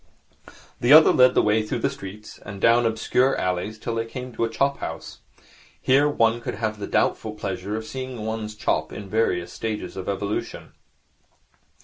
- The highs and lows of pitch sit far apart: No, narrow, 2.4 semitones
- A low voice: Yes, low, 110 Hz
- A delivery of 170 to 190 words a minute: Yes, average, 185 wpm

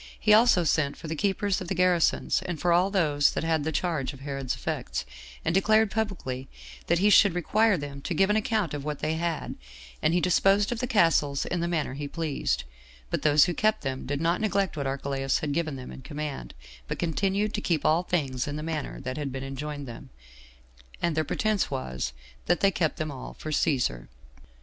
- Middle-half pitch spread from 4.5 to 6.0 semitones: Yes, average, 5.1 semitones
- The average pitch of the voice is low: No, medium, 160 Hz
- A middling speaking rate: No, fast, 210 wpm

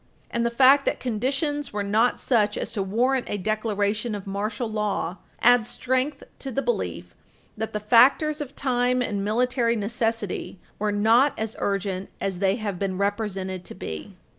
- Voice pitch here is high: Yes, high, 220 Hz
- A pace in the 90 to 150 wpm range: No, average, 165 wpm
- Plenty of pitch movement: No, average, 3.5 semitones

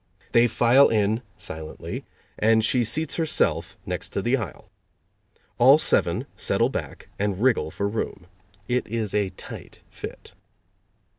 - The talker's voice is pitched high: No, low, 115 Hz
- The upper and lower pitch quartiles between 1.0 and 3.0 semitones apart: No, average, 3.4 semitones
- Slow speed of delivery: Yes, slow, 130 wpm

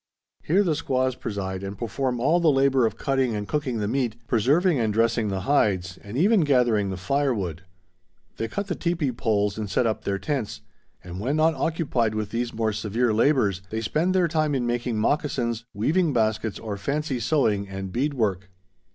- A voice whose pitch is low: Yes, low, 120 Hz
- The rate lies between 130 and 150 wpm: No, average, 185 wpm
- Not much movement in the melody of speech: No, wide, 5.5 semitones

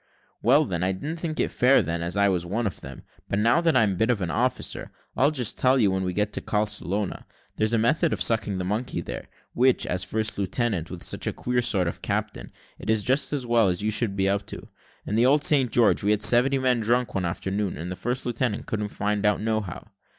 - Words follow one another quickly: Yes, fast, 250 wpm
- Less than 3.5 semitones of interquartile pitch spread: No, average, 4.1 semitones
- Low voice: Yes, low, 110 Hz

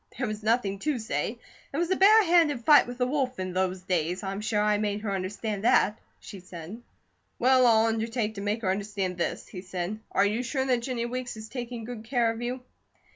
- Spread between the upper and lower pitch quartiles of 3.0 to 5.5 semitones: Yes, average, 3.9 semitones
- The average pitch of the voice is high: Yes, high, 220 Hz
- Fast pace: Yes, fast, 220 wpm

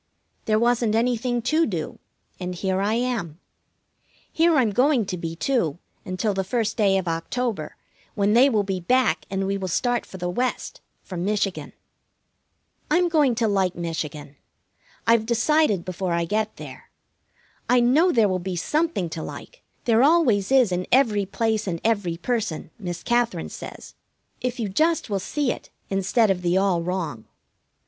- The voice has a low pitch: No, high, 210 Hz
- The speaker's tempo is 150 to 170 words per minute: Yes, average, 165 wpm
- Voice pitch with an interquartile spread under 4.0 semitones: No, average, 5.1 semitones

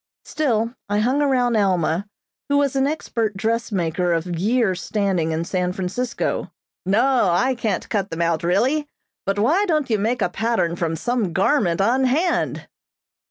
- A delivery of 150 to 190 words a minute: Yes, average, 160 wpm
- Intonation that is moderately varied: No, wide, 5.9 semitones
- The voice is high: Yes, high, 215 Hz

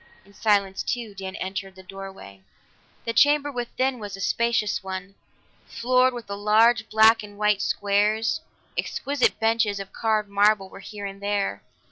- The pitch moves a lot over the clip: No, average, 2.7 semitones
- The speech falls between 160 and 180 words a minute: No, average, 150 wpm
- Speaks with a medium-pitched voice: No, high, 210 Hz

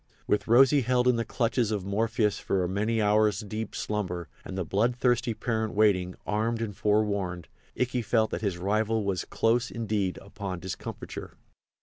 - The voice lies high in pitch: No, low, 105 Hz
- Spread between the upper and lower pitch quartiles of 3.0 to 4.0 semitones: No, narrow, 2.6 semitones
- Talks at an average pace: Yes, average, 160 wpm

